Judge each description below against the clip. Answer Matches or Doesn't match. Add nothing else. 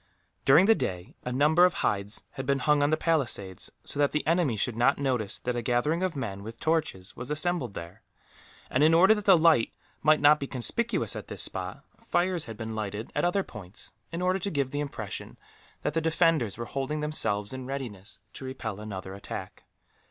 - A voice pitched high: Doesn't match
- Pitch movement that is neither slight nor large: Doesn't match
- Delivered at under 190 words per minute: Doesn't match